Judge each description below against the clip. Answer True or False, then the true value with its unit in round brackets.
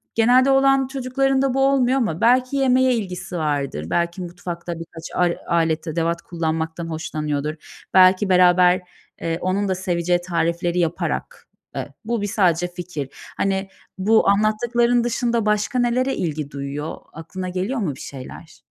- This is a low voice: False (185 Hz)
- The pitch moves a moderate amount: False (6.2 semitones)